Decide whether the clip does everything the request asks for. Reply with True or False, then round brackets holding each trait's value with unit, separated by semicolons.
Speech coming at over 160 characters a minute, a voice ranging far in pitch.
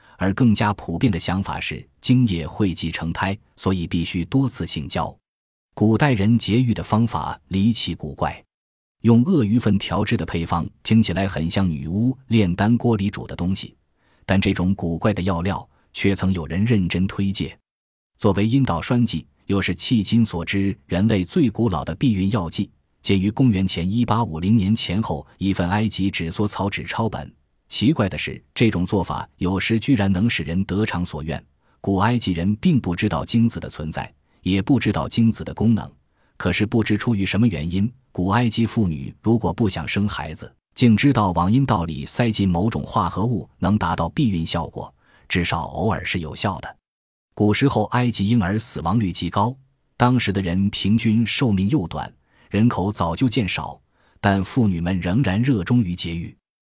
False (265 characters per minute; 4.6 semitones)